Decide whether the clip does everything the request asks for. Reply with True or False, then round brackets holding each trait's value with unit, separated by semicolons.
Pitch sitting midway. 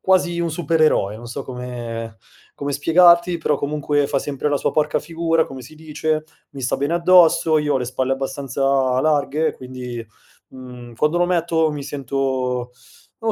True (145 Hz)